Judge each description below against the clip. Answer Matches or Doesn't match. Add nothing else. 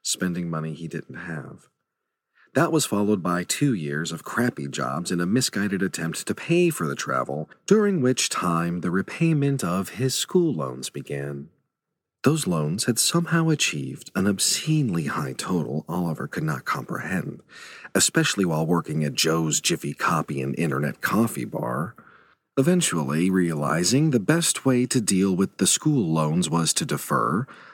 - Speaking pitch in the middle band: Doesn't match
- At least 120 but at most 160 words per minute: Matches